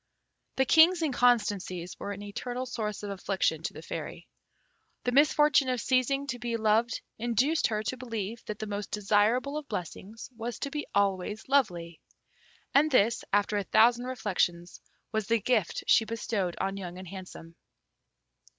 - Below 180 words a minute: Yes, average, 160 wpm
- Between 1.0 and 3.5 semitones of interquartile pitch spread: No, average, 4.1 semitones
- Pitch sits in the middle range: No, high, 220 Hz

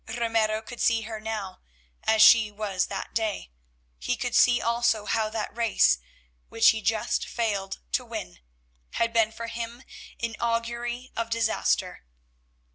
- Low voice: No, high, 225 Hz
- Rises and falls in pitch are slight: Yes, narrow, 1.3 semitones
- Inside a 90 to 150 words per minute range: Yes, average, 145 wpm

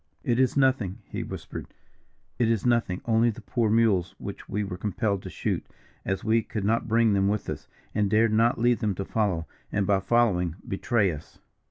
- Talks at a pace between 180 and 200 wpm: Yes, average, 195 wpm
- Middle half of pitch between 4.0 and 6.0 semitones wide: No, average, 3.1 semitones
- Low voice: Yes, low, 110 Hz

